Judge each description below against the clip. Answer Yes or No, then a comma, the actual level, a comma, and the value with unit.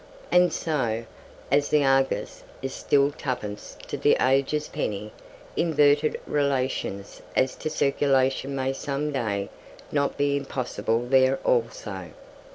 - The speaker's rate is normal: No, slow, 120 wpm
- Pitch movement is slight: Yes, narrow, 2.0 semitones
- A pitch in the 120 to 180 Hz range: Yes, low, 135 Hz